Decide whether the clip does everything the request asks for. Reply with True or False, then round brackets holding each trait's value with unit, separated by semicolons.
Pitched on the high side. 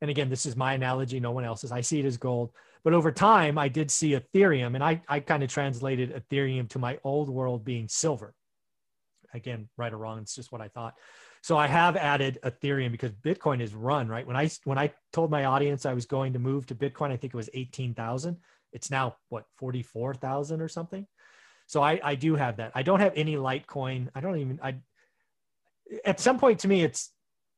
False (135 Hz)